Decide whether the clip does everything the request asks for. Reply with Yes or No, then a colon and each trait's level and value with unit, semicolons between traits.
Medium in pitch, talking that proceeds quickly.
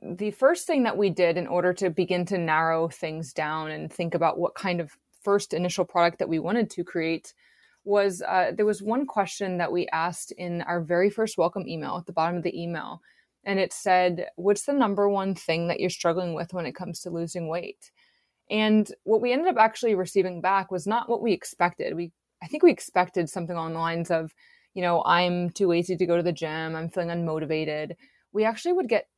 Yes: medium, 180 Hz; fast, 220 wpm